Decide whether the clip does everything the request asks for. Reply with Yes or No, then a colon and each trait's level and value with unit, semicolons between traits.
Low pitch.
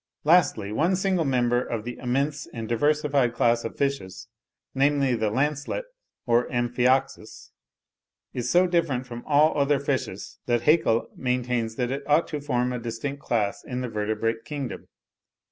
Yes: low, 125 Hz